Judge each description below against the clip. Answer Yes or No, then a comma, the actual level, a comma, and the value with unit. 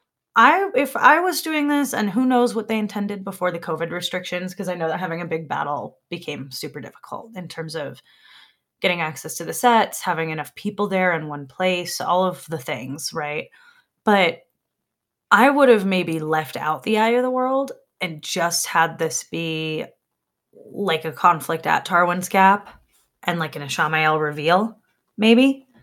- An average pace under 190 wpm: Yes, average, 175 wpm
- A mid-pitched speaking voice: Yes, medium, 180 Hz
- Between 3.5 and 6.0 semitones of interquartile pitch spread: Yes, average, 5.2 semitones